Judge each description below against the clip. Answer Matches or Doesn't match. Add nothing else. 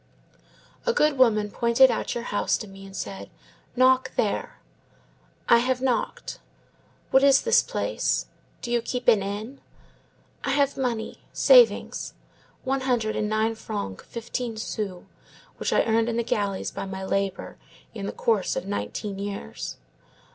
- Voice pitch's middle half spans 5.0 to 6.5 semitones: Doesn't match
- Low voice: Doesn't match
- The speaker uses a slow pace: Doesn't match